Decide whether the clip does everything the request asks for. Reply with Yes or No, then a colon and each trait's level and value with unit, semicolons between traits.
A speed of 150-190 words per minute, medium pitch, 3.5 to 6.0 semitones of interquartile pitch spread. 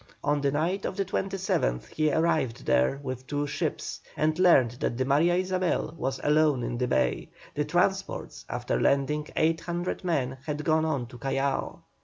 Yes: average, 170 wpm; medium, 150 Hz; average, 4.0 semitones